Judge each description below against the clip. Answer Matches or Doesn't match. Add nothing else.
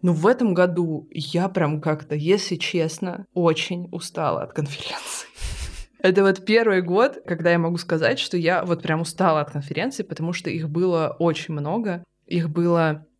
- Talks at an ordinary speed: Doesn't match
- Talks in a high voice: Doesn't match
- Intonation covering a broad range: Doesn't match